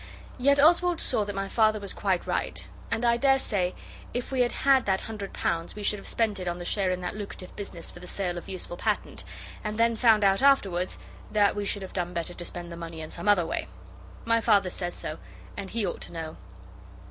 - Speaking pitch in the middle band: No, high, 200 Hz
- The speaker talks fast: Yes, fast, 230 wpm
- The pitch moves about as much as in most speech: Yes, average, 4.2 semitones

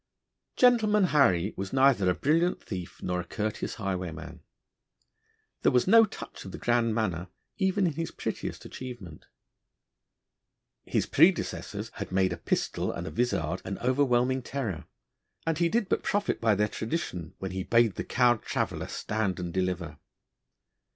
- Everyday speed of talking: Yes, average, 150 wpm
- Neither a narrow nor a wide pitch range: No, wide, 7.2 semitones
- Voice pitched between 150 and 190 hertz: No, low, 110 Hz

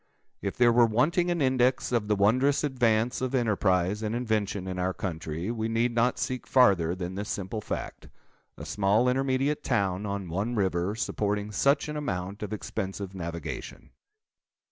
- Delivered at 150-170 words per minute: Yes, average, 160 wpm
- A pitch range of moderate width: Yes, average, 4.5 semitones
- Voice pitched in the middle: No, low, 105 Hz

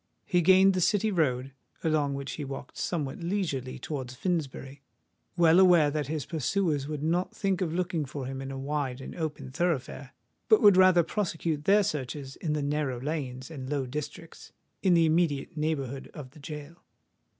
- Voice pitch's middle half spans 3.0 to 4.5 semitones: Yes, average, 4.1 semitones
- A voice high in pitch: No, medium, 150 Hz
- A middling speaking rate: Yes, average, 170 wpm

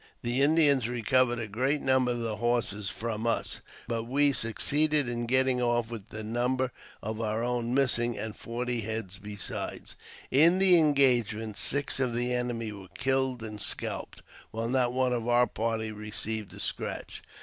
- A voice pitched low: Yes, low, 120 Hz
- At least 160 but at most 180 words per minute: Yes, average, 165 wpm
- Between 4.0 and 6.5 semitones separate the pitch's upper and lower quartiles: No, average, 2.7 semitones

